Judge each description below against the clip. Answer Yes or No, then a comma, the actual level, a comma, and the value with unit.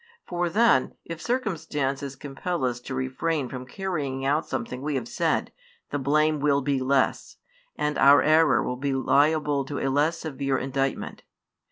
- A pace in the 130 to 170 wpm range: Yes, average, 160 wpm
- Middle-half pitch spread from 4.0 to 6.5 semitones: No, average, 2.7 semitones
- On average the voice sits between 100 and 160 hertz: Yes, medium, 140 Hz